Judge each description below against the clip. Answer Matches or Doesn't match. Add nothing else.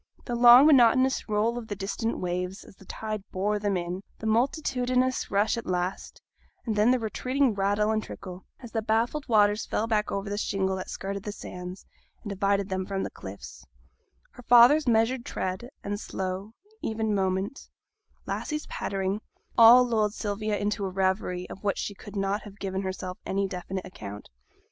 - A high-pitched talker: Matches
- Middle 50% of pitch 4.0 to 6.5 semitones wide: Doesn't match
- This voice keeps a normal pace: Matches